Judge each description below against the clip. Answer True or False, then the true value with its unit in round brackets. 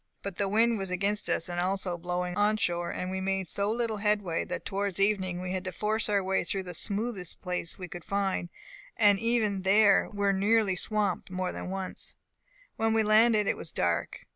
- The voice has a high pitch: True (195 Hz)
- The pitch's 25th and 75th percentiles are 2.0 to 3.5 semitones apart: True (2.4 semitones)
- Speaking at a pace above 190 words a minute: True (200 wpm)